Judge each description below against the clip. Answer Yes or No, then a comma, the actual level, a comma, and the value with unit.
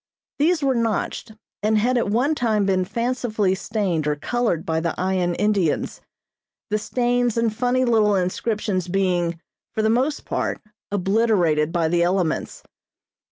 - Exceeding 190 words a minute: No, average, 145 wpm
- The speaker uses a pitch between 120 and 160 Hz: No, high, 210 Hz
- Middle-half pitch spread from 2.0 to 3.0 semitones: No, average, 4.8 semitones